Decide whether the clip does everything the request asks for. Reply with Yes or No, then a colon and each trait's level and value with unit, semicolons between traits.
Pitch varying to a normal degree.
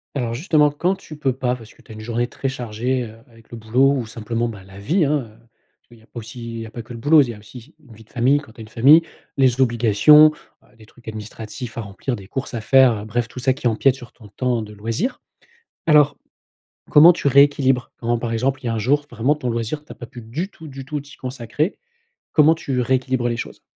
Yes: average, 3.5 semitones